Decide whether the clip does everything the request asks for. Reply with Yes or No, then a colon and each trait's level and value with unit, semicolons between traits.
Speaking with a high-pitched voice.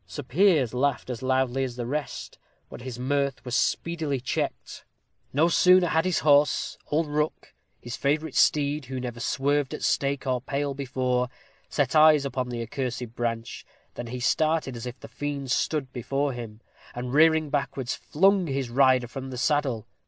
No: low, 135 Hz